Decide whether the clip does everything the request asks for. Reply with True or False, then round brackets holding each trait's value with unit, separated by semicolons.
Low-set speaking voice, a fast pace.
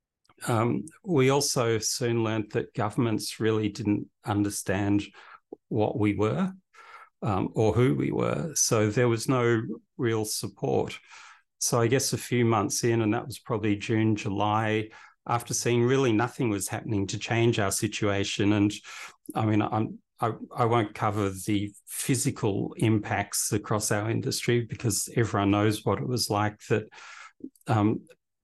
False (110 Hz; 150 wpm)